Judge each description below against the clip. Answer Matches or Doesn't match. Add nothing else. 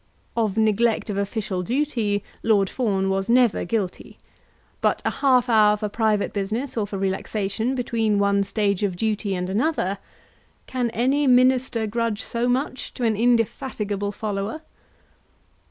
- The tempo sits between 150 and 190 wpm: Doesn't match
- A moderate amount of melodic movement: Matches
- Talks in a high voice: Matches